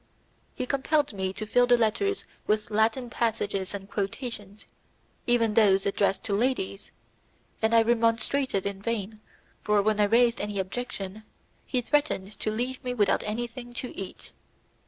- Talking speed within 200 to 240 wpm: No, average, 150 wpm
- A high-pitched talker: Yes, high, 220 Hz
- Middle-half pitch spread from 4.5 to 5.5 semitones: No, average, 3.2 semitones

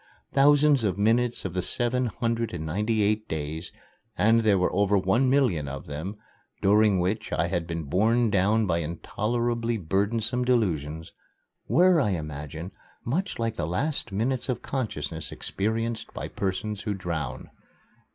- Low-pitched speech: Yes, low, 105 Hz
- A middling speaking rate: Yes, average, 150 wpm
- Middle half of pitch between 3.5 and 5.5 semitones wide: Yes, average, 5.2 semitones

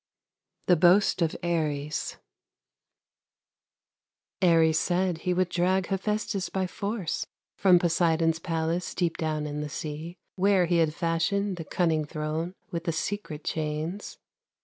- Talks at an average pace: No, slow, 125 wpm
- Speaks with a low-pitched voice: No, medium, 170 Hz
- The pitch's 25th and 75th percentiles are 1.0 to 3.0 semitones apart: Yes, narrow, 2.5 semitones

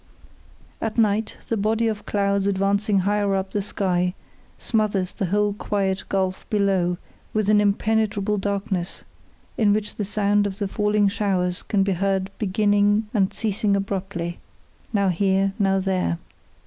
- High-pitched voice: Yes, high, 200 Hz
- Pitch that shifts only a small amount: Yes, narrow, 1.4 semitones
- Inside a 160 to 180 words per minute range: No, average, 145 wpm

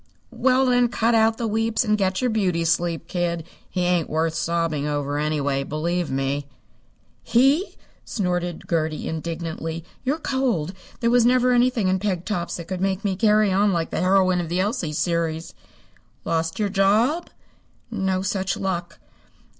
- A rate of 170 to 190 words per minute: No, average, 160 wpm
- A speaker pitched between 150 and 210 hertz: Yes, medium, 185 Hz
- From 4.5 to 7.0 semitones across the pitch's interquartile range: Yes, average, 4.8 semitones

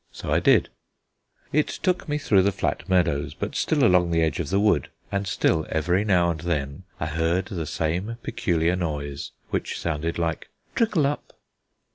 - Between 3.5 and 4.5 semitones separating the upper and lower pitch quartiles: Yes, average, 3.9 semitones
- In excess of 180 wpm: No, average, 175 wpm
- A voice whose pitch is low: Yes, very low, 85 Hz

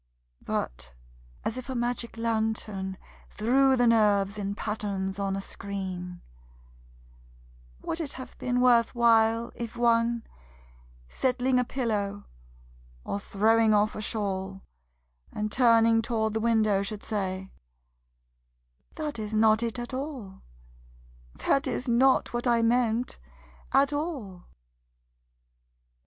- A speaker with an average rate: No, slow, 115 wpm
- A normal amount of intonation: Yes, average, 3.0 semitones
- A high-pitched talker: Yes, high, 225 Hz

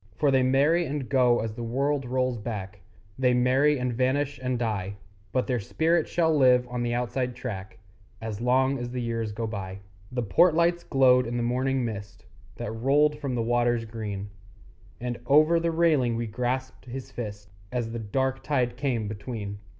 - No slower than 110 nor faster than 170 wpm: No, average, 180 wpm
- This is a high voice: No, low, 125 Hz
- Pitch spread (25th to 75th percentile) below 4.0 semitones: Yes, average, 2.8 semitones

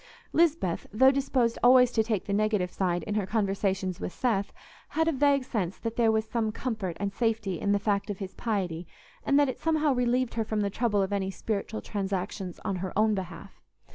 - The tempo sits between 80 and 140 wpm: No, fast, 205 wpm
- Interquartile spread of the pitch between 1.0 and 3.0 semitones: No, average, 3.8 semitones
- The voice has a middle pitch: No, high, 215 Hz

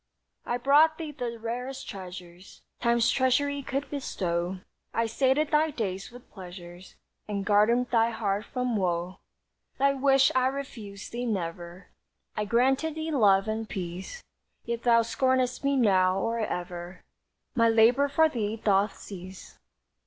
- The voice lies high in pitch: Yes, high, 230 Hz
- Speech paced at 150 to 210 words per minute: No, average, 140 wpm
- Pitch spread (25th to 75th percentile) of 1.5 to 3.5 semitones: No, average, 5.3 semitones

